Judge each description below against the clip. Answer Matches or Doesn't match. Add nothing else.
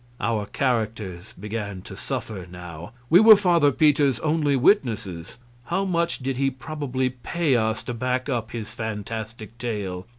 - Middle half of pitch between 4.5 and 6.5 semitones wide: Matches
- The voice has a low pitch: Matches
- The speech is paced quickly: Doesn't match